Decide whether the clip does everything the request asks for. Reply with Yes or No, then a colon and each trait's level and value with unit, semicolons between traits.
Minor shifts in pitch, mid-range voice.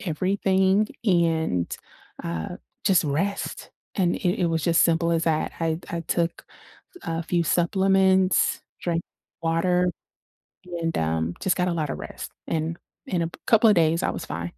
Yes: narrow, 2.3 semitones; medium, 170 Hz